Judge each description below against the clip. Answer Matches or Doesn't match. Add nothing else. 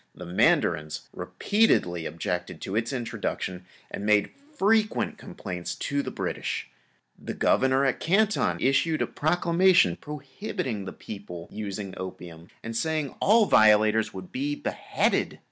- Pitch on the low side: Matches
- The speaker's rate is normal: Doesn't match